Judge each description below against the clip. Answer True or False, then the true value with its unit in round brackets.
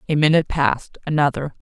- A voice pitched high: False (150 Hz)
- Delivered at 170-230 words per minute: False (110 wpm)